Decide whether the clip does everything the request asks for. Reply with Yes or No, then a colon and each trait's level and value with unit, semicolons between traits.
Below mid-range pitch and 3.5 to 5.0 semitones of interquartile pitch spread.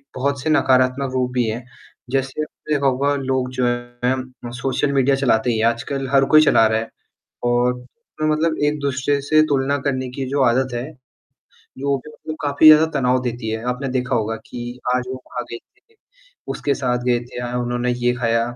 No: low, 130 Hz; narrow, 2.4 semitones